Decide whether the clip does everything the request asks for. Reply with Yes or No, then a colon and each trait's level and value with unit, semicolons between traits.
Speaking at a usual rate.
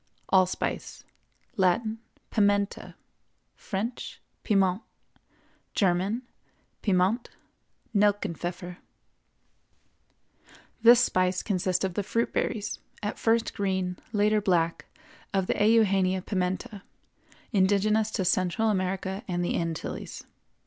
No: slow, 80 wpm